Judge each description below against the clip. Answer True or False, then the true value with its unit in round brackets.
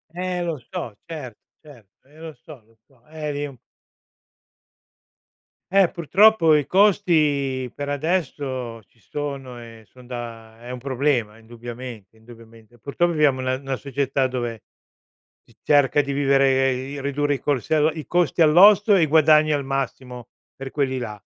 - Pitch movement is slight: False (3.9 semitones)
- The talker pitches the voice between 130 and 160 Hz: True (135 Hz)